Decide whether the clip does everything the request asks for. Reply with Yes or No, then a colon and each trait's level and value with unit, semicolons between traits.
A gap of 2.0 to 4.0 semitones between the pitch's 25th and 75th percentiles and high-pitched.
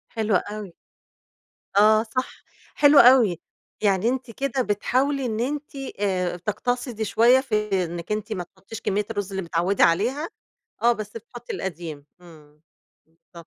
No: average, 4.9 semitones; high, 210 Hz